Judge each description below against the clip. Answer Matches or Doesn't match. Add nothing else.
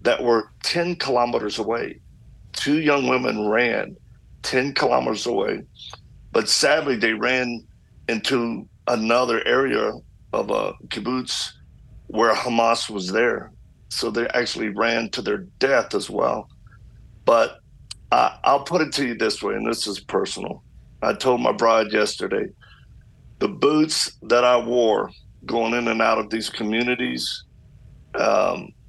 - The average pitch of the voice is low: Matches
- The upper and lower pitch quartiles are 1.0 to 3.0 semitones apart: Matches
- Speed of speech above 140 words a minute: Doesn't match